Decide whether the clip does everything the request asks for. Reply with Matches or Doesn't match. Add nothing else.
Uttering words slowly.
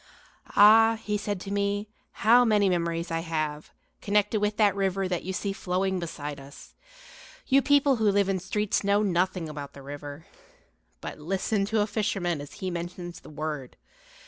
Doesn't match